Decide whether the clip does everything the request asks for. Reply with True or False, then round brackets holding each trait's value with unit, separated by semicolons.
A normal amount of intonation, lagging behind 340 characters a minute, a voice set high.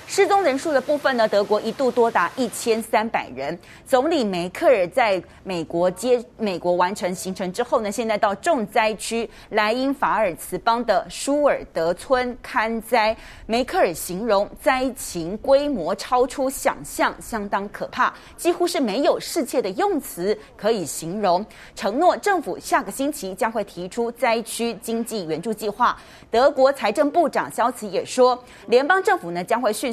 True (4.9 semitones; 250 characters per minute; 230 Hz)